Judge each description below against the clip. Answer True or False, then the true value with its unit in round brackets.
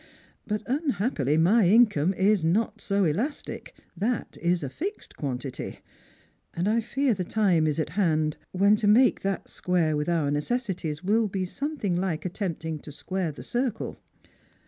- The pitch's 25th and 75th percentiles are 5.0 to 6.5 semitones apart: True (5.5 semitones)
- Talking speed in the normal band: True (165 wpm)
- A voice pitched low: False (190 Hz)